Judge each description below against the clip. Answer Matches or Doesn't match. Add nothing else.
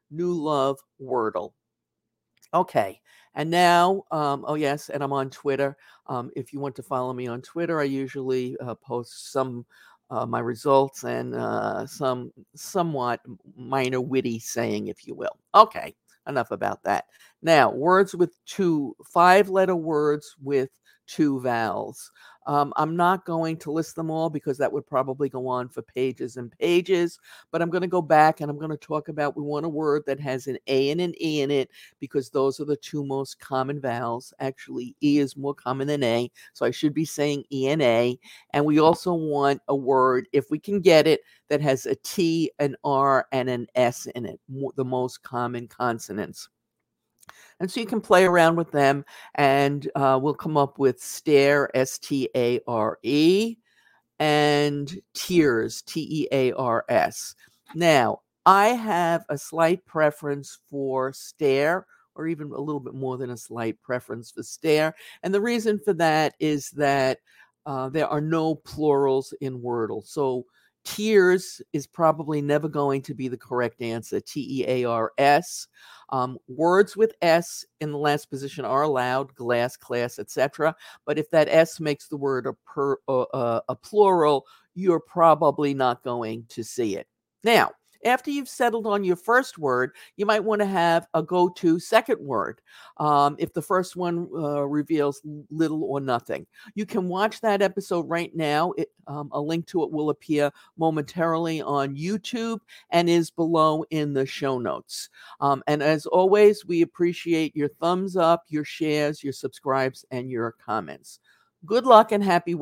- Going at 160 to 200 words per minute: Matches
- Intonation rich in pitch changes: Doesn't match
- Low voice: Doesn't match